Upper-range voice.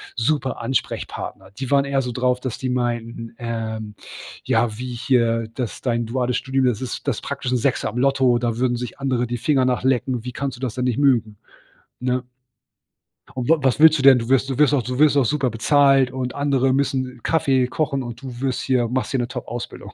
No: low, 125 Hz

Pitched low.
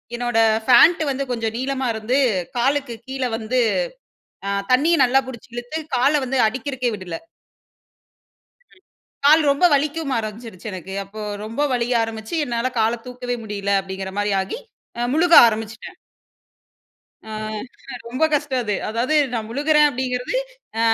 No: high, 245 Hz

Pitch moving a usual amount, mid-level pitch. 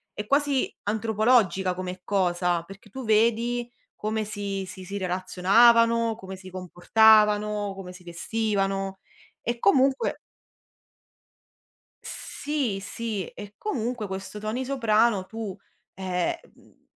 No: average, 3.3 semitones; high, 210 Hz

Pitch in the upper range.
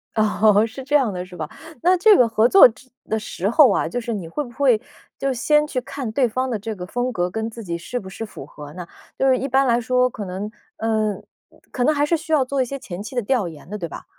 Yes: high, 230 Hz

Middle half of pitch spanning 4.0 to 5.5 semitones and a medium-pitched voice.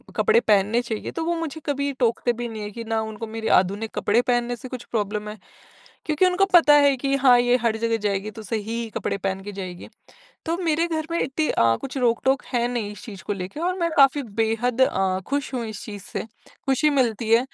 No: average, 4.7 semitones; high, 235 Hz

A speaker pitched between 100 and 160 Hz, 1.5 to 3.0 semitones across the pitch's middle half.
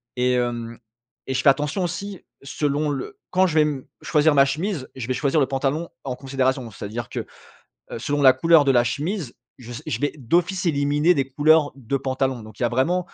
No: medium, 140 Hz; average, 3.4 semitones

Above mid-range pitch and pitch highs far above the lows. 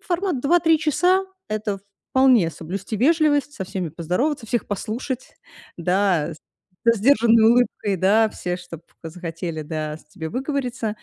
Yes: high, 215 Hz; wide, 7.1 semitones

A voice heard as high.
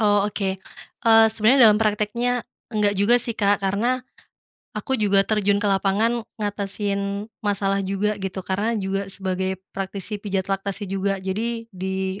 Yes: high, 200 Hz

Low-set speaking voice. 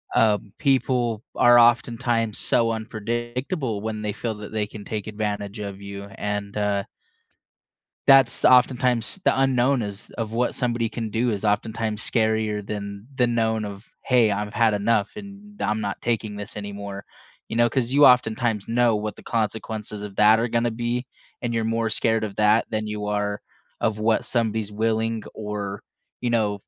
Yes: low, 110 Hz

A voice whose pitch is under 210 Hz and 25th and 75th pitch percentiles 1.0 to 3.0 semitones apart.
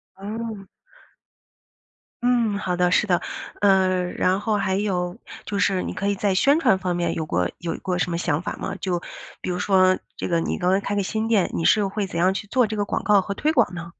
Yes: high, 195 Hz; narrow, 2.5 semitones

